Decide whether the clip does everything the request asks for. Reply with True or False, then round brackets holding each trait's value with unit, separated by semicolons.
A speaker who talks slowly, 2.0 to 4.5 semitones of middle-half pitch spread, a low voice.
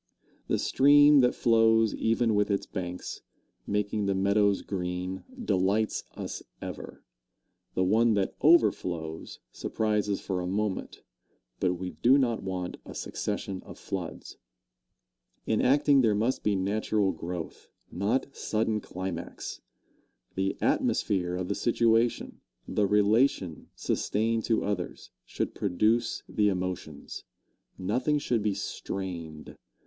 True (120 wpm; 3.4 semitones; 105 Hz)